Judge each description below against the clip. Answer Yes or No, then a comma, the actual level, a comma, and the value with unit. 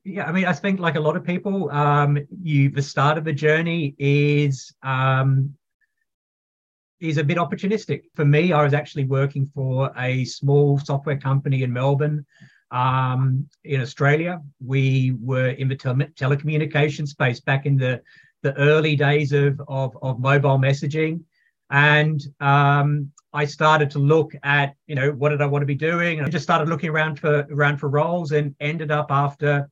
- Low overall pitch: No, medium, 145 Hz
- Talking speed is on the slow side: No, average, 175 wpm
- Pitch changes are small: Yes, narrow, 1.9 semitones